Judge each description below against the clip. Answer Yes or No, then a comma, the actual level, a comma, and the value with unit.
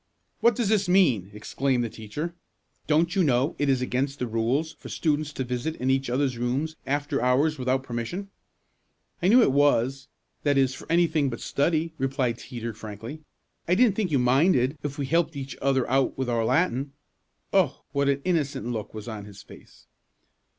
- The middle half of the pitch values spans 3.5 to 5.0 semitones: Yes, average, 4.3 semitones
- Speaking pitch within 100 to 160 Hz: Yes, low, 135 Hz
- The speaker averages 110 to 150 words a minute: No, average, 180 wpm